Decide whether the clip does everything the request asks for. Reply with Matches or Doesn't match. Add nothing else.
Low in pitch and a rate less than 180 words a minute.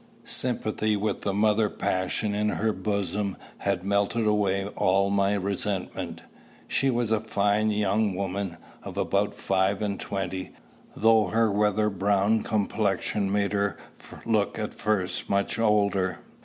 Matches